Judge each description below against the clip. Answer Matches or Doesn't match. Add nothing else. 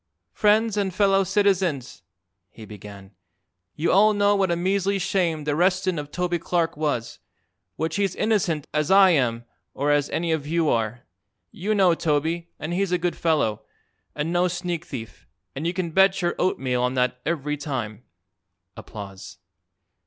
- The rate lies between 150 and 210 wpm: Matches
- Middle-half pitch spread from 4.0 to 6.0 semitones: Matches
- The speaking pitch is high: Doesn't match